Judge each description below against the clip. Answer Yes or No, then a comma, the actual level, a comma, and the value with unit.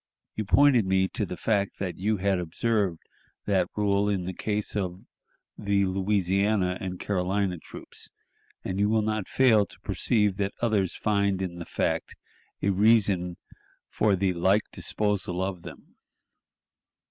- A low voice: Yes, low, 100 Hz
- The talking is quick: No, average, 145 wpm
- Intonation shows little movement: Yes, narrow, 2.2 semitones